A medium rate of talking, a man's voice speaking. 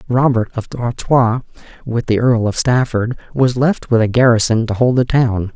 Yes: average, 185 wpm; male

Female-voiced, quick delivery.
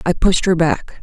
Yes: female; fast, 235 wpm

